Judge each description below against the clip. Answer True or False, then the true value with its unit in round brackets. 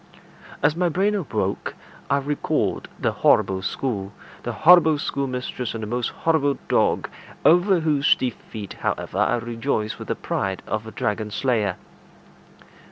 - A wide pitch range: True (6.2 semitones)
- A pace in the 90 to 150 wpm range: True (140 wpm)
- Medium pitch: False (125 Hz)